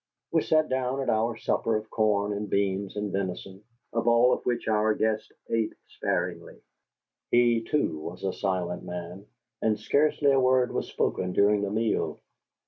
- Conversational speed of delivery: Yes, average, 165 wpm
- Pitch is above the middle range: No, low, 110 Hz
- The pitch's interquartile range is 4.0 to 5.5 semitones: No, average, 3.4 semitones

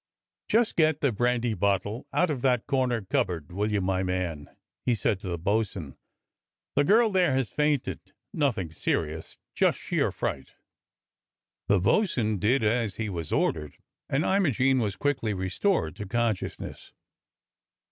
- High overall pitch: No, low, 110 Hz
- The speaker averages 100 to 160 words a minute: Yes, average, 155 wpm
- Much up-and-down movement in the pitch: Yes, wide, 6.3 semitones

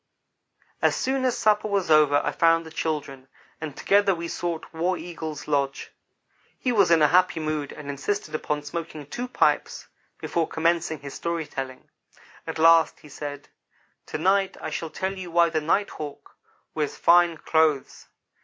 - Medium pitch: Yes, medium, 160 Hz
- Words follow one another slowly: No, average, 165 wpm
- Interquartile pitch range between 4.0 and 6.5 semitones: No, average, 2.8 semitones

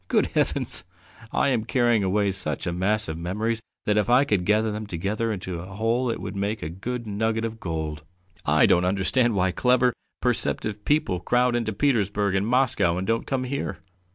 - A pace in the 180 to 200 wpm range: Yes, average, 190 wpm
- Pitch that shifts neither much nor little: Yes, average, 4.0 semitones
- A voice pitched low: Yes, low, 105 Hz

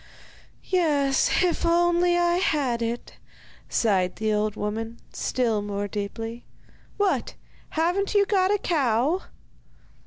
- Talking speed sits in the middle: No, slow, 115 wpm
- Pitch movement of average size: No, wide, 8.0 semitones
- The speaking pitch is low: No, very high, 275 Hz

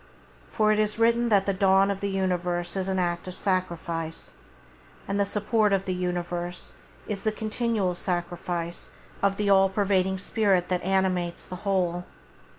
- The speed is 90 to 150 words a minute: No, average, 160 wpm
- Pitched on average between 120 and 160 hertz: No, high, 190 Hz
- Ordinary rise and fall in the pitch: No, narrow, 2.1 semitones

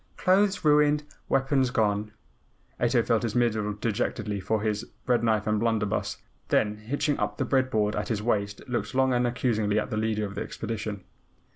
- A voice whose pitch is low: Yes, low, 110 Hz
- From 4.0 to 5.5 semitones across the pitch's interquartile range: No, average, 3.1 semitones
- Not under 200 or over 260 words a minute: No, average, 175 wpm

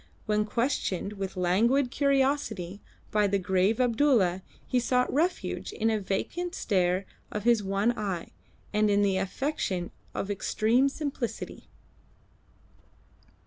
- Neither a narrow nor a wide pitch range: Yes, average, 4.5 semitones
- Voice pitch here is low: No, high, 210 Hz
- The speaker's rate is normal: No, slow, 120 wpm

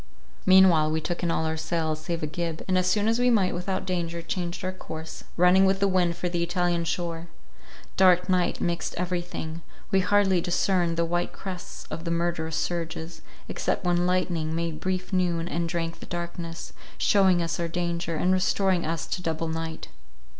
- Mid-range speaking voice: Yes, medium, 175 Hz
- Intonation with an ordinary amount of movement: No, narrow, 1.7 semitones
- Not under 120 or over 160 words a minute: No, average, 185 wpm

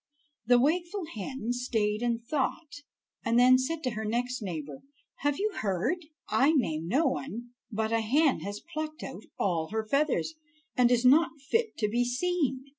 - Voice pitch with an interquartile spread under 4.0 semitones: No, wide, 5.4 semitones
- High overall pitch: Yes, very high, 250 Hz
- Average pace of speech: Yes, average, 170 wpm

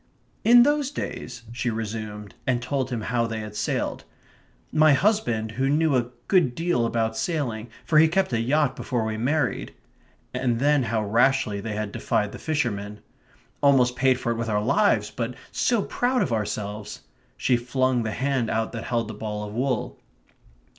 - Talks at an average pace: Yes, average, 180 wpm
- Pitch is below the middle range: Yes, low, 120 Hz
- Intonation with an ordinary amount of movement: Yes, average, 4.2 semitones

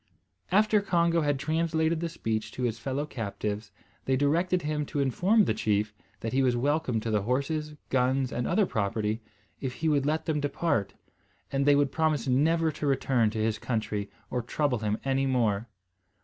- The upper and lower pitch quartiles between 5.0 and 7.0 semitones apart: Yes, wide, 5.6 semitones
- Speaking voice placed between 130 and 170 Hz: Yes, low, 135 Hz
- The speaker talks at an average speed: Yes, average, 180 wpm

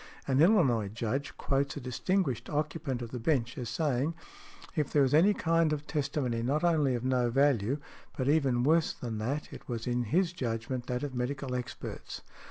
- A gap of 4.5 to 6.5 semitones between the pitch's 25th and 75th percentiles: No, average, 3.7 semitones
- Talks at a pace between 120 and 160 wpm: No, average, 180 wpm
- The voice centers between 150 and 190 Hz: No, low, 135 Hz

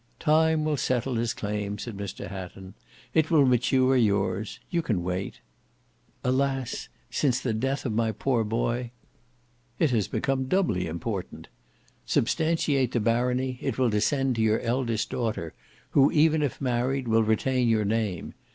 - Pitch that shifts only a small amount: No, average, 3.8 semitones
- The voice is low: Yes, low, 120 Hz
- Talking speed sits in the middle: Yes, average, 150 wpm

